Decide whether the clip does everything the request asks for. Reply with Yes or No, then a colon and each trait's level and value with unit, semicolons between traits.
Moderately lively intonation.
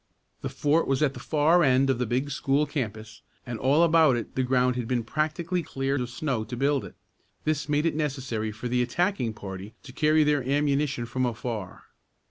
Yes: average, 3.7 semitones